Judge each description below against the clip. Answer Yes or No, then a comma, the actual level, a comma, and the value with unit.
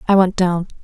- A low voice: No, medium, 185 Hz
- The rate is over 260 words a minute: No, fast, 215 wpm